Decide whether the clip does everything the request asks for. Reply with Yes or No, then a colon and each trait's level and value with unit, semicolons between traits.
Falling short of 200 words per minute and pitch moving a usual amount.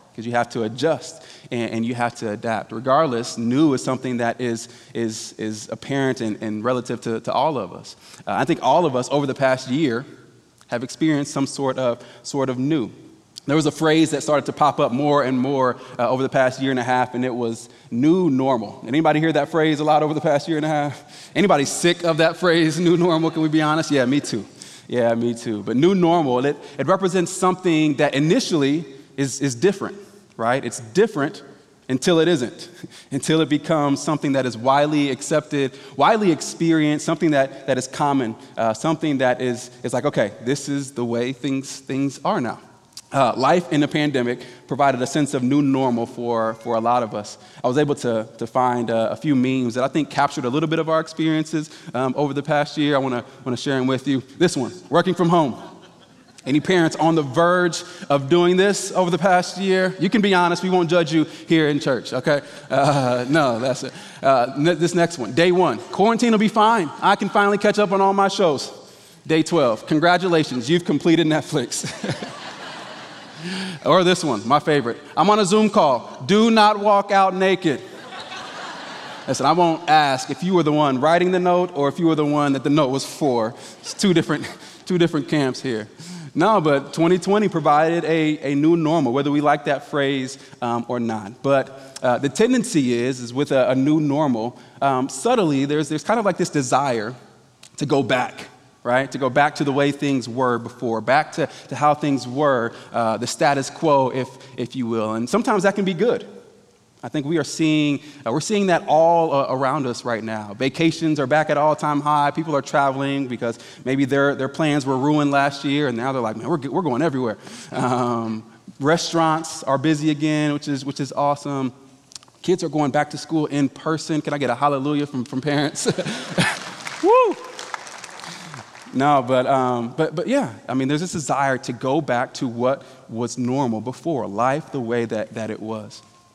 No: fast, 205 wpm; average, 4.2 semitones